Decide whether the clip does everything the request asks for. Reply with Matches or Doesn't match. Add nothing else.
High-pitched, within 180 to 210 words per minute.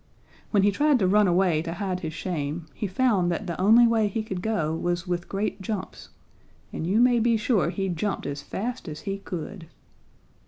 Matches